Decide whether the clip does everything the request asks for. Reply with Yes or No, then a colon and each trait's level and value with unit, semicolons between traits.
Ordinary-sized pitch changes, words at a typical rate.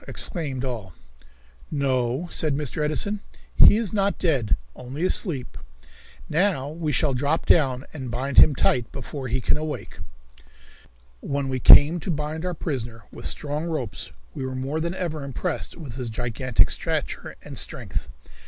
Yes: average, 3.9 semitones; average, 155 wpm